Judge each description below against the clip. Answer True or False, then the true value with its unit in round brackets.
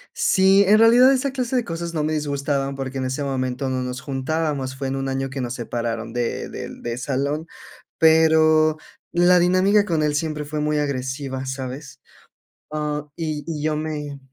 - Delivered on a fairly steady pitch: False (3.3 semitones)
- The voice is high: False (150 Hz)